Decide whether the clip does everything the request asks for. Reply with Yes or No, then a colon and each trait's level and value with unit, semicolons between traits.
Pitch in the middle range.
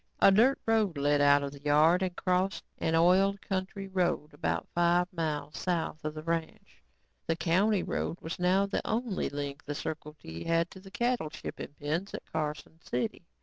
Yes: medium, 170 Hz